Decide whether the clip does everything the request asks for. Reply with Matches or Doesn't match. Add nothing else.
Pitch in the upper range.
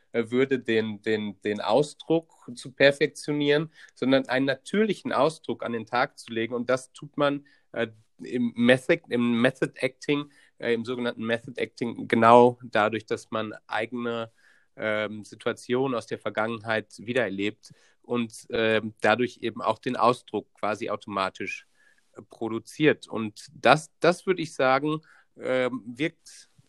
Doesn't match